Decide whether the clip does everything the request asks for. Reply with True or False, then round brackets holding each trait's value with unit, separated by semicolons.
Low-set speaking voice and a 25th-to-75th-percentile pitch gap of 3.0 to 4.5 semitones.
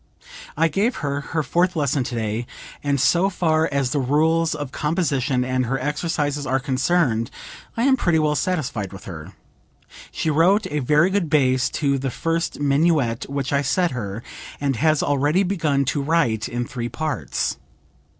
False (145 Hz; 4.1 semitones)